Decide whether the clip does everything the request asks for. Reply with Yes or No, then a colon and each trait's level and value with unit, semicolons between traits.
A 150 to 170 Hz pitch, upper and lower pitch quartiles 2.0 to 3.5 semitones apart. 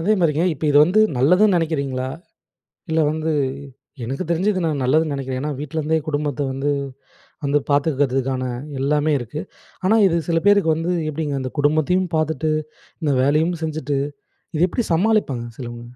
Yes: medium, 155 Hz; average, 2.9 semitones